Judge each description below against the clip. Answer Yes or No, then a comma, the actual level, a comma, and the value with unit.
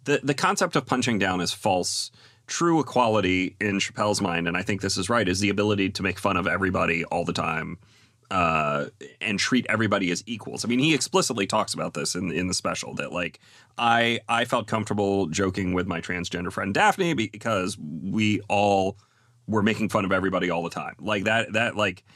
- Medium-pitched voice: No, low, 105 Hz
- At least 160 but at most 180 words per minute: No, average, 200 wpm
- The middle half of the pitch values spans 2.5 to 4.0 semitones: Yes, average, 3.7 semitones